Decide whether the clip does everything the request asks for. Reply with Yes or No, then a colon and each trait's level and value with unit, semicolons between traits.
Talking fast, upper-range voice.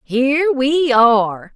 No: slow, 115 wpm; very high, 260 Hz